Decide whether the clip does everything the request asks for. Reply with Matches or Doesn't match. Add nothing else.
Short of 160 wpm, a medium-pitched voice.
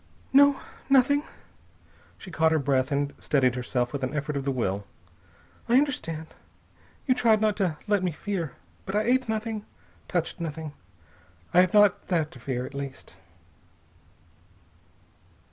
Matches